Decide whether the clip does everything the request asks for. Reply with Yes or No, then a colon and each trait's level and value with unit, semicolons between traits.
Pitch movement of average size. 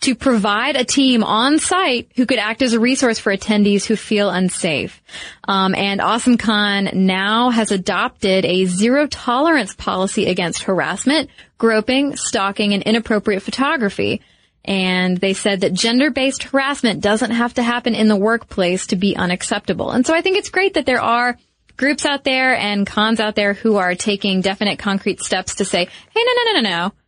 Yes: average, 4.3 semitones